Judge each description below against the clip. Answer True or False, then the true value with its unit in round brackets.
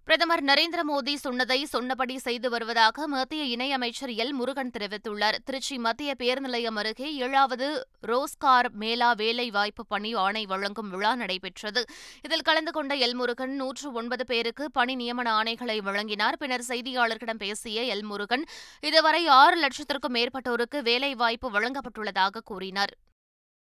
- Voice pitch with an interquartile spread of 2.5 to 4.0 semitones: True (3.5 semitones)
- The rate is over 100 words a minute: True (125 wpm)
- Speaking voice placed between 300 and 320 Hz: False (245 Hz)